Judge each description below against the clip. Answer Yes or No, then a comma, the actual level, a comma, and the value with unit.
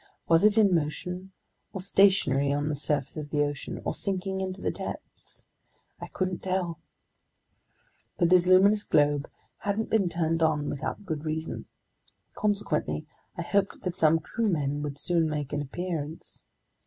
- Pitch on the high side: No, medium, 165 Hz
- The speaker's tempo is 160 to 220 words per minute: No, average, 150 wpm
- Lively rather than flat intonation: No, average, 4.4 semitones